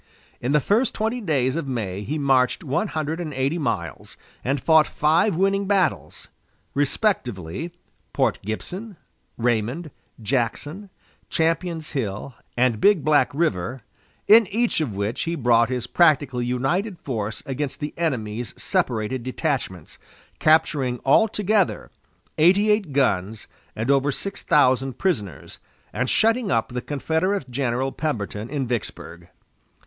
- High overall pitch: No, medium, 140 Hz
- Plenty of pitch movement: Yes, wide, 6.0 semitones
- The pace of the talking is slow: Yes, slow, 130 wpm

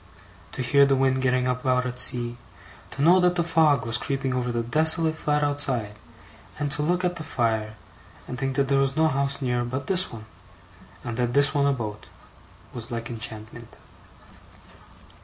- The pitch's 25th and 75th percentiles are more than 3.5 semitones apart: No, average, 3.2 semitones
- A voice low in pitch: Yes, low, 130 Hz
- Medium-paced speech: Yes, average, 180 wpm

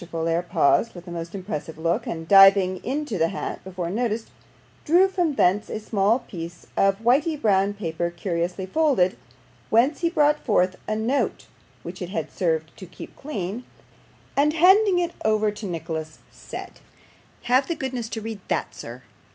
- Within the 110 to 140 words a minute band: No, average, 165 wpm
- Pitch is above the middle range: Yes, high, 200 Hz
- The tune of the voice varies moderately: No, wide, 6.8 semitones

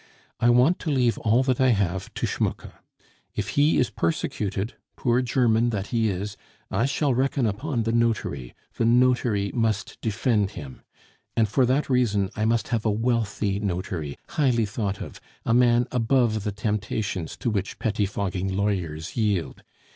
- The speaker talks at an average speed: Yes, average, 160 wpm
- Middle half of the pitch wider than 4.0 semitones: No, average, 3.5 semitones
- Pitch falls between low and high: No, low, 110 Hz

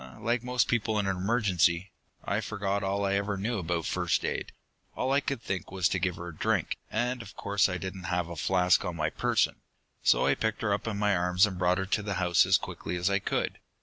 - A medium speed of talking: No, fast, 245 wpm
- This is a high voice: No, very low, 95 Hz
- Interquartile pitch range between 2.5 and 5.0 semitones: Yes, average, 2.9 semitones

